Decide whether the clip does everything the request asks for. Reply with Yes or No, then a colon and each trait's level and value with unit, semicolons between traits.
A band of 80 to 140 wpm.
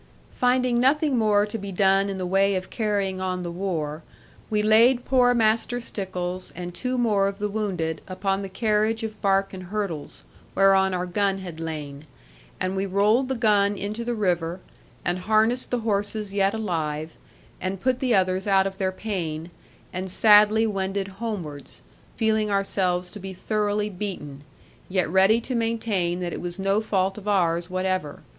No: average, 170 wpm